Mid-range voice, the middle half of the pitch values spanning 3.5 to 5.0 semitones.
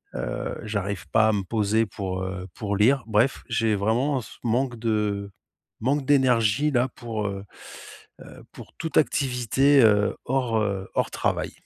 No: low, 110 Hz; average, 4.1 semitones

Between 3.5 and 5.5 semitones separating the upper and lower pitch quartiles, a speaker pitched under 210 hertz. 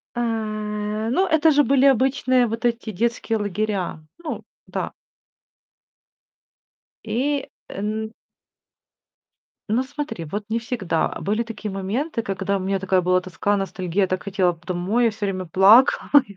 No: average, 4.4 semitones; high, 215 Hz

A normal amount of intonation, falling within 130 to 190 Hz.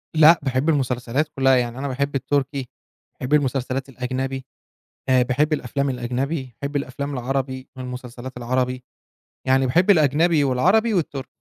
No: narrow, 2.1 semitones; low, 135 Hz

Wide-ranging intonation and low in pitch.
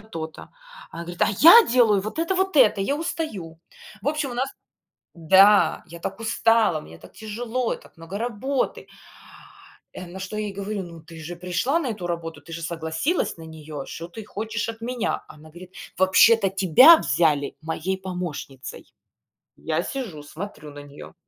No: wide, 5.8 semitones; high, 190 Hz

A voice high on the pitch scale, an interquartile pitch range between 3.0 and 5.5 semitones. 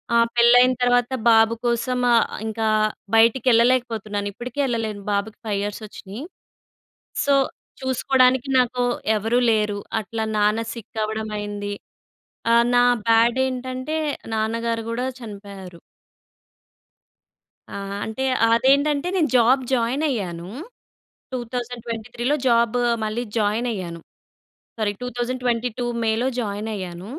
No: high, 230 Hz; narrow, 2.6 semitones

